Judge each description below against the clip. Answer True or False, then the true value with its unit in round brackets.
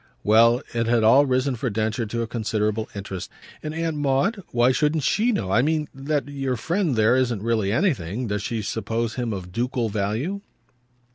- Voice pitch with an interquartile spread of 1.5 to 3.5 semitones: False (4.4 semitones)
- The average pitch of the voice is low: True (120 Hz)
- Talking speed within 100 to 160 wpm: False (185 wpm)